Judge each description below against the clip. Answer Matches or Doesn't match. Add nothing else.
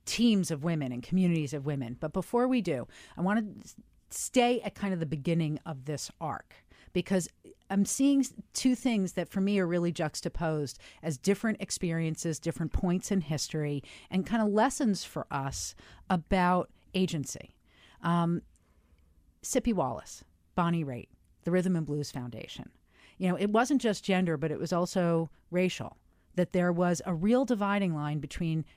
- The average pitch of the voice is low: Doesn't match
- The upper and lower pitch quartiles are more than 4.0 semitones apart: Matches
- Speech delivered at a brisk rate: Doesn't match